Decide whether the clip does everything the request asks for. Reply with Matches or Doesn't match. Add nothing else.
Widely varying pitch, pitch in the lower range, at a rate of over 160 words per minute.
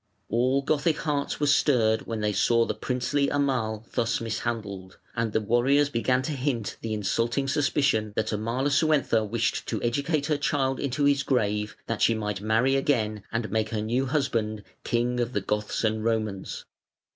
Doesn't match